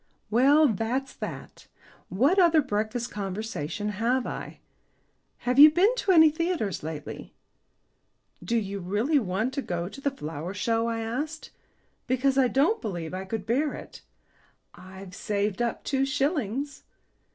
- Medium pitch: No, high, 235 Hz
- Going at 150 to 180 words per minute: No, average, 140 wpm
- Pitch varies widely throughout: Yes, wide, 5.9 semitones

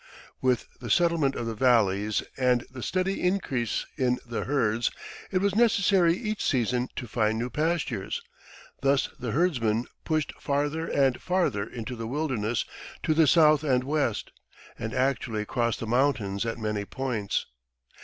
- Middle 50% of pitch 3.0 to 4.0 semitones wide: No, average, 5.3 semitones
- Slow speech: No, average, 150 wpm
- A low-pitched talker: Yes, low, 130 Hz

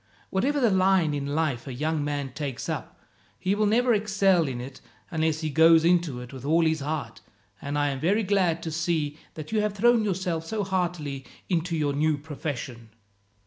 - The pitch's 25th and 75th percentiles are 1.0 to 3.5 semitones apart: No, average, 4.7 semitones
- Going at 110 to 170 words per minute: No, average, 190 wpm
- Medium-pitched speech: Yes, medium, 160 Hz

